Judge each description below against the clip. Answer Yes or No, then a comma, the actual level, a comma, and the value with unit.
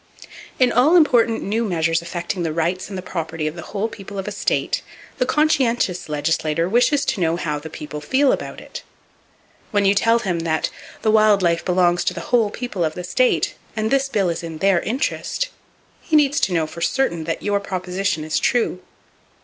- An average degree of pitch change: No, wide, 5.8 semitones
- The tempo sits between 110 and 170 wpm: No, average, 200 wpm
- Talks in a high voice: Yes, high, 195 Hz